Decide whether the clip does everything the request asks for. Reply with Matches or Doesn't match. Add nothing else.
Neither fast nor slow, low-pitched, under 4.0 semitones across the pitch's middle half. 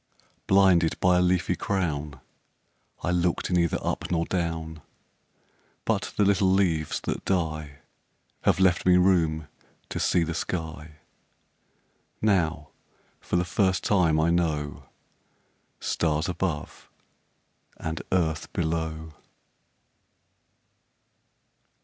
Doesn't match